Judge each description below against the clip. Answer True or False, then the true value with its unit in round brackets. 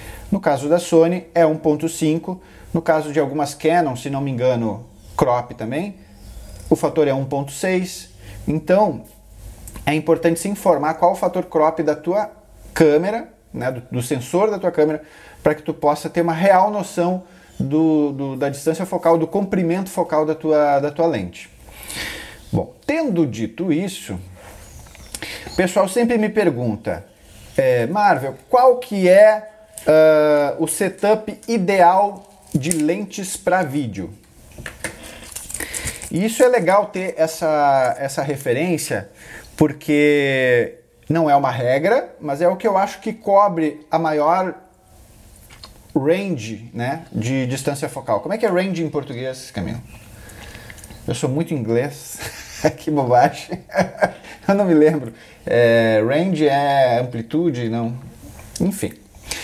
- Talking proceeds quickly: False (135 wpm)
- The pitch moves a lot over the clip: True (5.9 semitones)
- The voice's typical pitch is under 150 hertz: False (155 Hz)